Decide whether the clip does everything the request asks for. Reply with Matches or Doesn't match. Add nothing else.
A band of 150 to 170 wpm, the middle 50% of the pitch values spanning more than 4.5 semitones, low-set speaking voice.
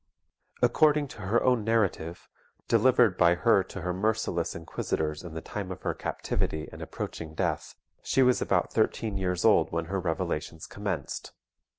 Matches